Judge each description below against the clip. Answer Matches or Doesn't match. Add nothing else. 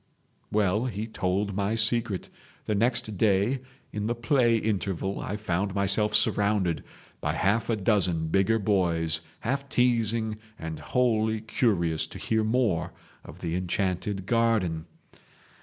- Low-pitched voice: Matches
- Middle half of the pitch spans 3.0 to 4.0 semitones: Matches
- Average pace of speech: Doesn't match